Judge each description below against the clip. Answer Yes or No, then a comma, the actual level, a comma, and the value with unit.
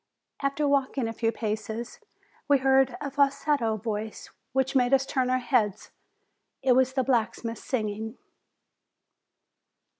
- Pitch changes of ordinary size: Yes, average, 3.3 semitones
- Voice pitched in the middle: No, very high, 255 Hz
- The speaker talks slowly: Yes, slow, 130 wpm